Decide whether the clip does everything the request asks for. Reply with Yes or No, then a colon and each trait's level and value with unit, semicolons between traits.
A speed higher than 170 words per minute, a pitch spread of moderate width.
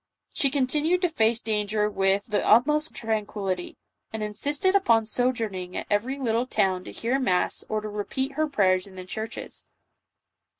No: average, 160 wpm; average, 4.6 semitones